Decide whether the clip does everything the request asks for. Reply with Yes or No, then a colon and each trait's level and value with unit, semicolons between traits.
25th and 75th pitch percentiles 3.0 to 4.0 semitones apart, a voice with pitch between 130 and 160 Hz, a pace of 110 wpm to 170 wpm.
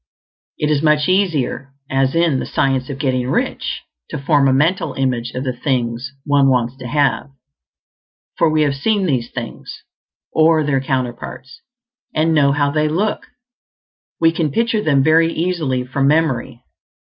Yes: average, 3.4 semitones; medium, 140 Hz; average, 160 wpm